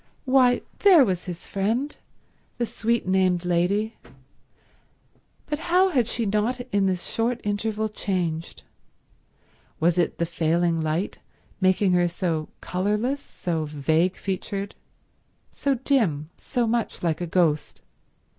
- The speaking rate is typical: No, slow, 120 wpm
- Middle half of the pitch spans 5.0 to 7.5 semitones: Yes, wide, 5.4 semitones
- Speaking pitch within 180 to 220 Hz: Yes, high, 190 Hz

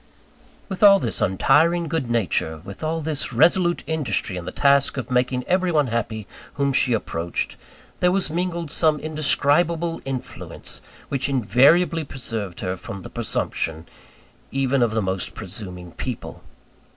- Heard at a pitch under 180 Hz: Yes, low, 135 Hz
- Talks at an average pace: Yes, average, 145 wpm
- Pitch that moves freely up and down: Yes, wide, 7.0 semitones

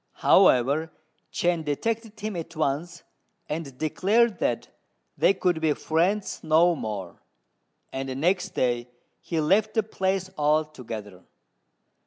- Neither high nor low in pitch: Yes, medium, 160 Hz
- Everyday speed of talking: No, slow, 115 wpm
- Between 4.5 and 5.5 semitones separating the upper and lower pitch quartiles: Yes, average, 5.1 semitones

